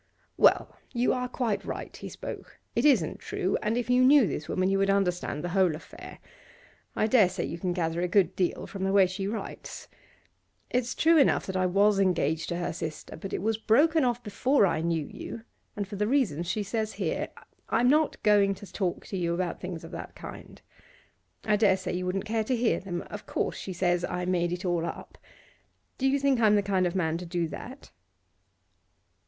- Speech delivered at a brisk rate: Yes, fast, 210 wpm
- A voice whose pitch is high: Yes, high, 195 Hz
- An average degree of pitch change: Yes, average, 4.1 semitones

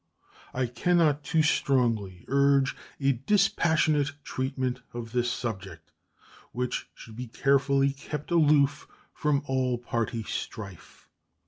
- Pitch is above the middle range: No, low, 135 Hz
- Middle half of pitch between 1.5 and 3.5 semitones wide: Yes, average, 3.2 semitones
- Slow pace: Yes, slow, 115 wpm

